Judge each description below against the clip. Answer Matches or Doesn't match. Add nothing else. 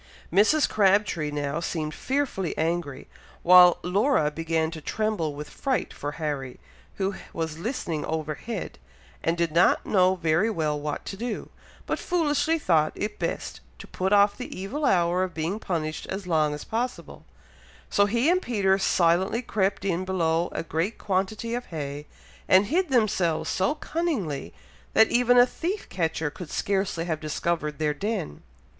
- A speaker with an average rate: Matches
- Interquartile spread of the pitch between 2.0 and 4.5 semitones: Doesn't match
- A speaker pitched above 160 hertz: Matches